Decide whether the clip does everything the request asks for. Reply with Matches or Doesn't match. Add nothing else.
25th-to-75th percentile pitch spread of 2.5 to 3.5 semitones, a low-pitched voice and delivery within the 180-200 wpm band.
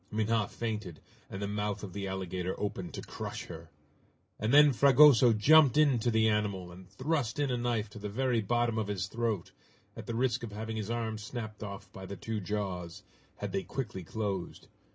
Matches